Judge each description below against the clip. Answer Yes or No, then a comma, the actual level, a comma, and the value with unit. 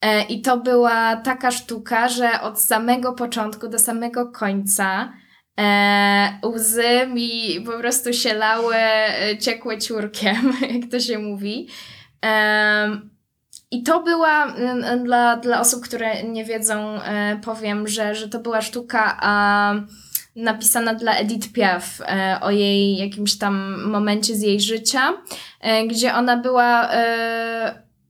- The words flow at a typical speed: Yes, average, 130 wpm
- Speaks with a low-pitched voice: No, high, 225 Hz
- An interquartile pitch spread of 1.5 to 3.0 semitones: Yes, narrow, 2.4 semitones